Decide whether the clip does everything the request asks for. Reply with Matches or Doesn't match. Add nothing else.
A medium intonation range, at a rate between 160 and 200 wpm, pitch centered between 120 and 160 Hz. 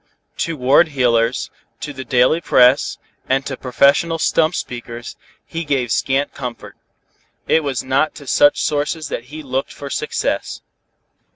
Doesn't match